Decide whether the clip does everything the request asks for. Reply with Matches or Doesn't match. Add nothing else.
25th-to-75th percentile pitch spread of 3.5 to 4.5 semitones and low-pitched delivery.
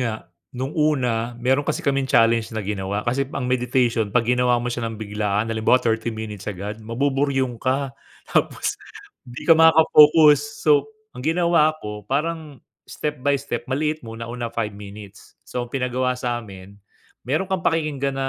Matches